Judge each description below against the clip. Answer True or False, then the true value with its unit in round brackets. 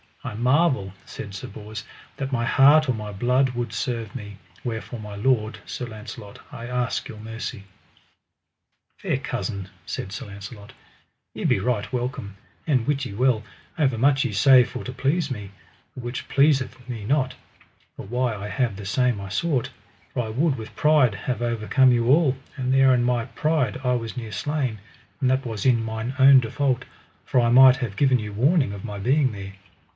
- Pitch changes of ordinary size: True (3.6 semitones)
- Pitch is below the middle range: True (120 Hz)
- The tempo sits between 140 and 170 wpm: False (185 wpm)